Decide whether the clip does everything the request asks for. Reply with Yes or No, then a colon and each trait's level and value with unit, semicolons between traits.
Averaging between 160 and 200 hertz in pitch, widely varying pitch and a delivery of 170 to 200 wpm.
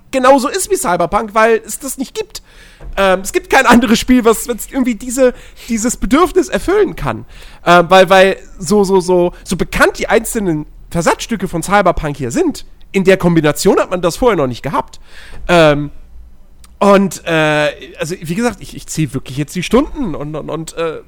Yes: high, 190 Hz; wide, 7.4 semitones; average, 180 wpm